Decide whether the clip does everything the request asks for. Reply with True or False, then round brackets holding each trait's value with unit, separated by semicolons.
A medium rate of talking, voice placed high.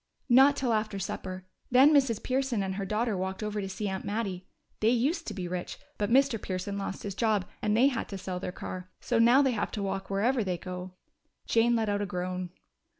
False (220 wpm; 205 Hz)